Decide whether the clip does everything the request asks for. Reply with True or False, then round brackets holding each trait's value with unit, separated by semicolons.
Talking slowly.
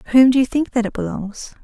False (295 wpm)